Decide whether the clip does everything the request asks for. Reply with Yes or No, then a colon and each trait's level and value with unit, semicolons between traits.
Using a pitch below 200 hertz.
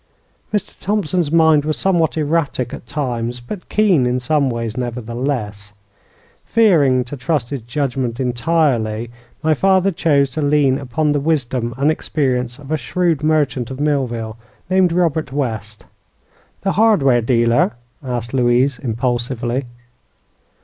Yes: low, 135 Hz